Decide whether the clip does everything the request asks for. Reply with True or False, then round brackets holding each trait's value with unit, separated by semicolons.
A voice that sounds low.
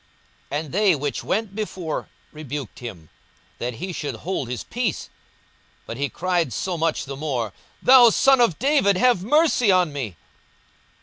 False (170 Hz)